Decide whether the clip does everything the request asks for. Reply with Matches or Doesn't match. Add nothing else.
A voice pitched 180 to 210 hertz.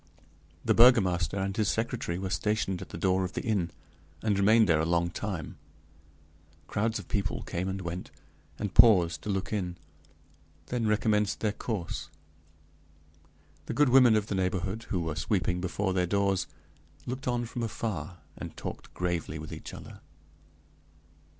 Doesn't match